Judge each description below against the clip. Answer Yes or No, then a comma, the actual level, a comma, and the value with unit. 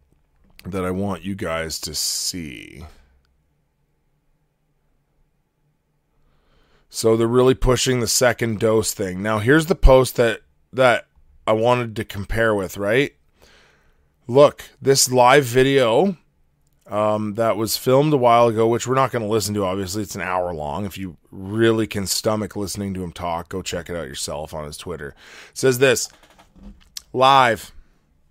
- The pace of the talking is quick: No, average, 150 wpm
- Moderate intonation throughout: No, wide, 5.8 semitones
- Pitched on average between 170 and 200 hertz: No, low, 110 Hz